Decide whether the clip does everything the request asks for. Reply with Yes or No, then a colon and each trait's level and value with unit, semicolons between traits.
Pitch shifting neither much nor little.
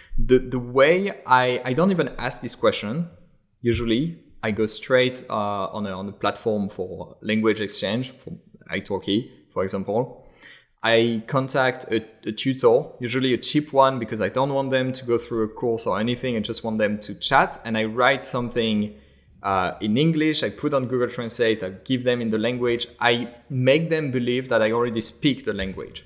Yes: average, 3.0 semitones